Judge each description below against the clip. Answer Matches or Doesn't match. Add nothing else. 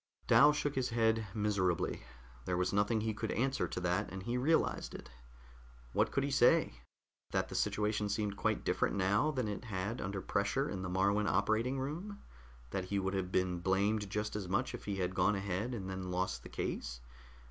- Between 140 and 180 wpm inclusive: Doesn't match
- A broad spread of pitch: Doesn't match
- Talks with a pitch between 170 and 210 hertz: Doesn't match